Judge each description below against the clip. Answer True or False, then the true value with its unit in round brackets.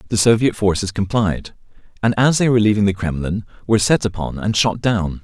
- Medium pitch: False (105 Hz)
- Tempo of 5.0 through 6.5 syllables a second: True (5.8 syllables/s)